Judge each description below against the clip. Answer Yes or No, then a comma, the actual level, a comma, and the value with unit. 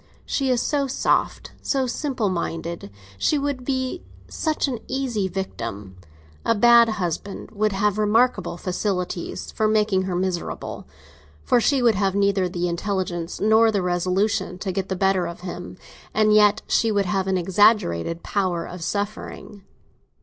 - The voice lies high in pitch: Yes, high, 200 Hz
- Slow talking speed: No, average, 150 wpm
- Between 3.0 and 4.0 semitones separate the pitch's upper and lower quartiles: Yes, average, 3.7 semitones